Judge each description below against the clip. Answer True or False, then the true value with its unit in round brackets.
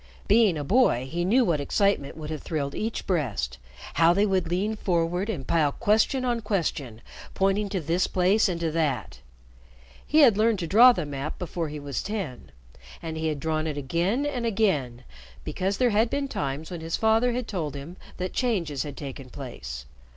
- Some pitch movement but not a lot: False (6.4 semitones)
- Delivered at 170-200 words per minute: True (190 wpm)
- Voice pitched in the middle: True (175 Hz)